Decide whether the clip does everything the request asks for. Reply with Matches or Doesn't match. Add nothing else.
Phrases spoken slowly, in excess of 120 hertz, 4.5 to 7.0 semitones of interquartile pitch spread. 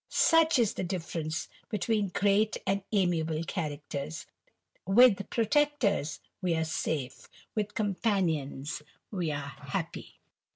Matches